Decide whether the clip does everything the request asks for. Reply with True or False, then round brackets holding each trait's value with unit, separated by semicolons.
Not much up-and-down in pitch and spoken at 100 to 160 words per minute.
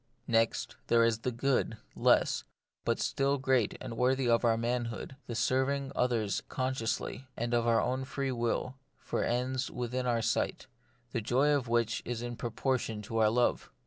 False (2.1 semitones; 170 wpm)